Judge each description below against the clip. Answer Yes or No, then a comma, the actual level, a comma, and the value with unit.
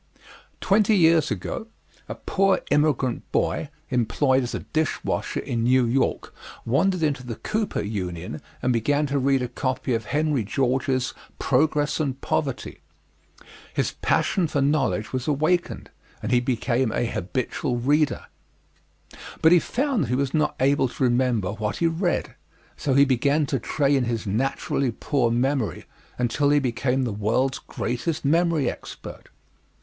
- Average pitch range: Yes, average, 3.7 semitones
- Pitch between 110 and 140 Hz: Yes, low, 135 Hz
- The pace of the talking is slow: No, average, 150 wpm